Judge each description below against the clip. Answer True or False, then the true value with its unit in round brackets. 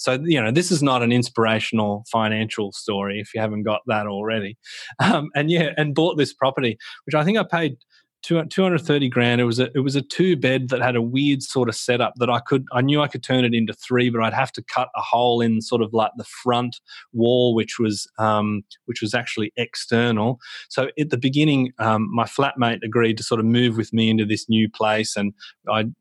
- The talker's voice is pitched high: False (120 Hz)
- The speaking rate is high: True (225 wpm)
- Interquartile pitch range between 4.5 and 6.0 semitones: False (3.3 semitones)